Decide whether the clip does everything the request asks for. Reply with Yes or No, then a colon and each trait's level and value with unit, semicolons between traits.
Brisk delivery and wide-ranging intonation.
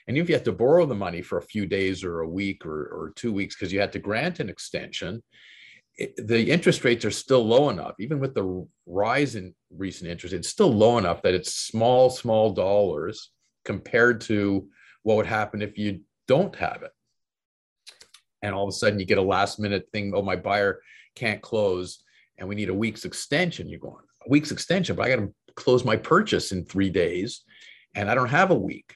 No: fast, 215 wpm; average, 3.2 semitones